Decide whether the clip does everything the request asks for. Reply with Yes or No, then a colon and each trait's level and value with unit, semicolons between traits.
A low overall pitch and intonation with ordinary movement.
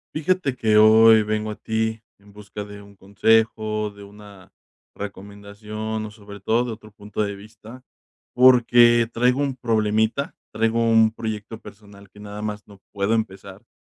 No: low, 110 Hz; narrow, 1.6 semitones